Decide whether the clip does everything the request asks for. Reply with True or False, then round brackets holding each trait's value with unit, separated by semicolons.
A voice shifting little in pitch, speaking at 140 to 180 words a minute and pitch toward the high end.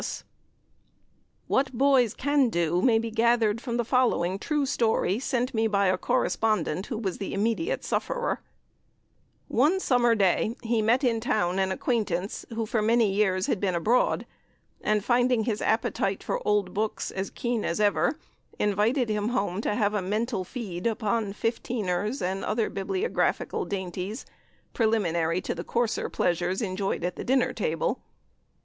False (3.8 semitones; 155 wpm; 215 Hz)